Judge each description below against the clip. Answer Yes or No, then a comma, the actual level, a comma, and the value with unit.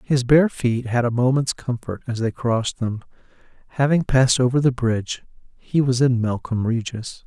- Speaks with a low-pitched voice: Yes, low, 125 Hz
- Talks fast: No, average, 175 wpm